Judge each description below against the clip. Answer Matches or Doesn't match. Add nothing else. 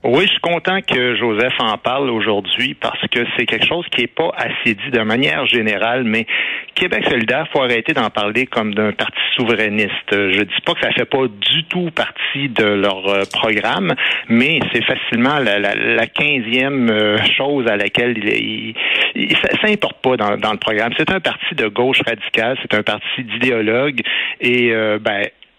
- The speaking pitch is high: Doesn't match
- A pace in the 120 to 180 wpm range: Doesn't match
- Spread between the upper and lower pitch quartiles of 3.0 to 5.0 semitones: Matches